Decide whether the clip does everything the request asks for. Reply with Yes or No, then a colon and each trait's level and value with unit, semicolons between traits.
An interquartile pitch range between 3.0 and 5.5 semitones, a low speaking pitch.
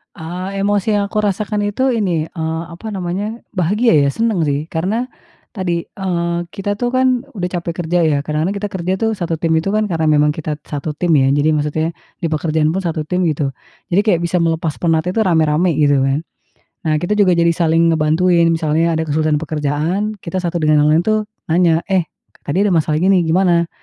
No: average, 3.5 semitones; medium, 170 Hz